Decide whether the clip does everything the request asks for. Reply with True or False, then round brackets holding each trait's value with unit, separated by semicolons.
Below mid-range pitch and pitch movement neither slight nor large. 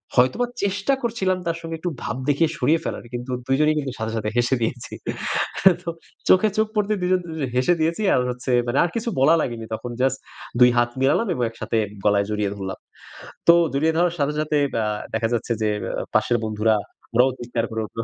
False (130 Hz; 6.5 semitones)